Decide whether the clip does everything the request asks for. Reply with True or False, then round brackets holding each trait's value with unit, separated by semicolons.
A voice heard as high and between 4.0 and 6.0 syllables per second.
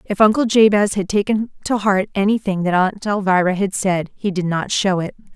True (200 Hz; 5.2 syllables/s)